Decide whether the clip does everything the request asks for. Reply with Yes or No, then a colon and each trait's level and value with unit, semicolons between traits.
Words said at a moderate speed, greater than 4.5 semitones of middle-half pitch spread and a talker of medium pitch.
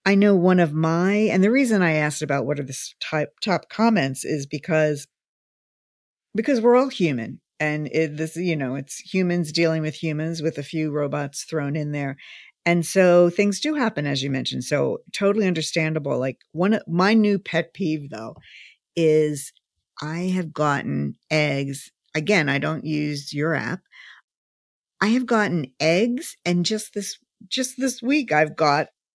Yes: average, 165 wpm; average, 5.1 semitones; medium, 160 Hz